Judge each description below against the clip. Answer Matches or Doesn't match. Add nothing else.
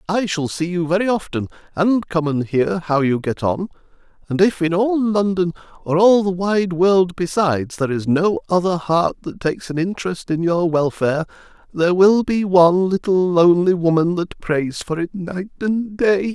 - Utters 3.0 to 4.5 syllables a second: Doesn't match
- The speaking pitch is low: Doesn't match